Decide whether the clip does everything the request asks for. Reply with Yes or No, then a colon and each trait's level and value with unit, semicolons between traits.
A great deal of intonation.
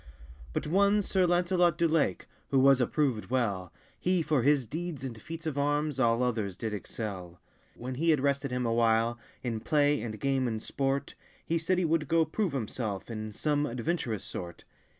Yes: wide, 5.7 semitones